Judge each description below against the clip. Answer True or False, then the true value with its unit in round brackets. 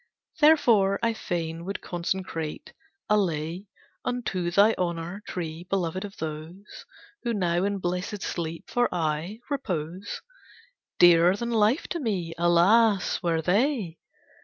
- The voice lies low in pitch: False (180 Hz)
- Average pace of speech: False (125 wpm)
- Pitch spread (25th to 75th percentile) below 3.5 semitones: False (3.8 semitones)